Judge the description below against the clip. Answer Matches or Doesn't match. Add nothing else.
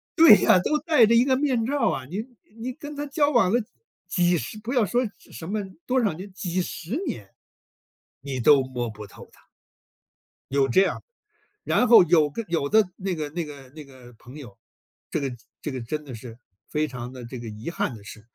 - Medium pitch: Matches